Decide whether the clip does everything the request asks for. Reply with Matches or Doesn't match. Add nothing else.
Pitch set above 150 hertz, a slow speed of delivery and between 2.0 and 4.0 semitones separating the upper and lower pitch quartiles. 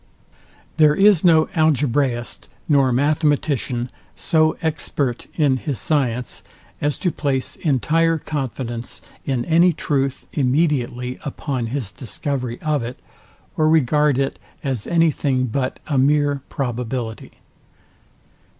Doesn't match